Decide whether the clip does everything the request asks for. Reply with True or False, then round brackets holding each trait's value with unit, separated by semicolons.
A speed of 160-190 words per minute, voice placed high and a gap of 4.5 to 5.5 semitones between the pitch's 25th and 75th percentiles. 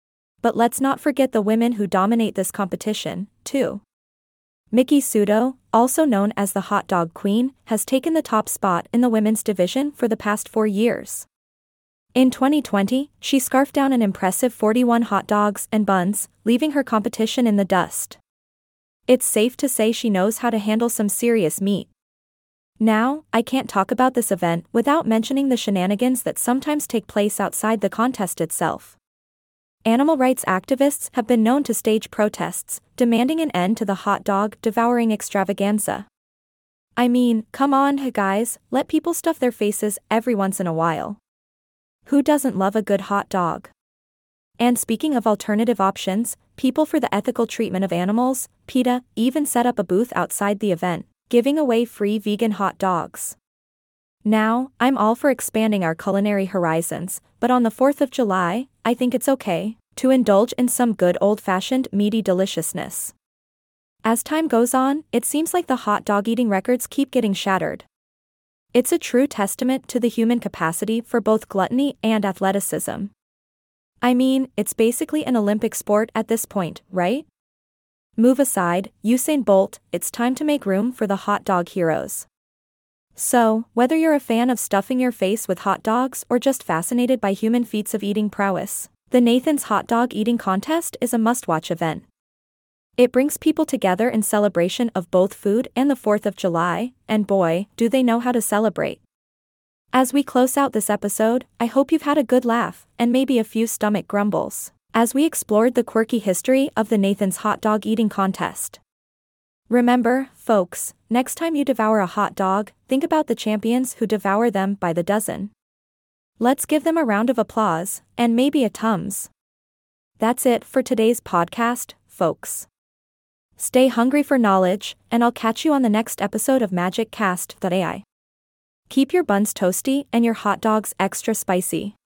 False (170 wpm; 225 Hz; 3.9 semitones)